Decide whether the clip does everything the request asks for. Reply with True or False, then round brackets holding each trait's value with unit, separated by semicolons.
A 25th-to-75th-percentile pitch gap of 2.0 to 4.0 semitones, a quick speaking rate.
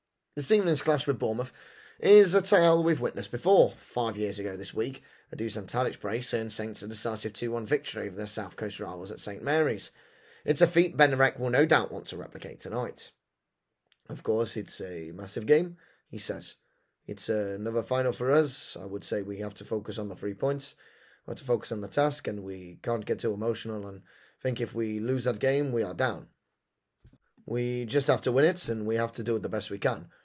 False (4.8 semitones; 215 wpm)